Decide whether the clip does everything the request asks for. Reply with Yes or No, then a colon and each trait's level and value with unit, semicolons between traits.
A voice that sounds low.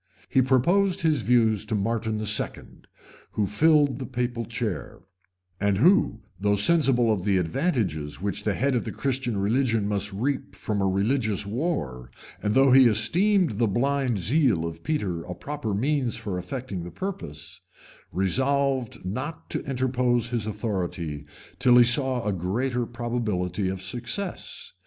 Yes: low, 115 Hz